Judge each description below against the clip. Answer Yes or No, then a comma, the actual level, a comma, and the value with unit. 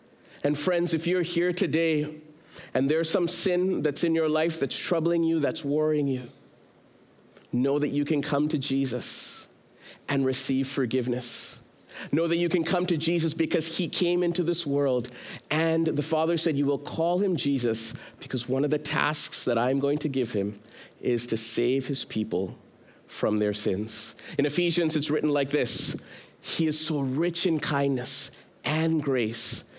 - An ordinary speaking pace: Yes, average, 170 wpm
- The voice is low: No, medium, 150 Hz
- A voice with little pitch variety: No, average, 3.9 semitones